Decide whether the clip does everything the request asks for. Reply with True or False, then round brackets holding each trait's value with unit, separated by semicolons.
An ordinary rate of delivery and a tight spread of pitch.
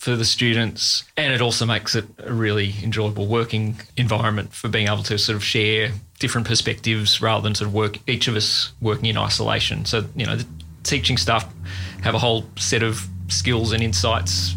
True (195 wpm; 1.8 semitones)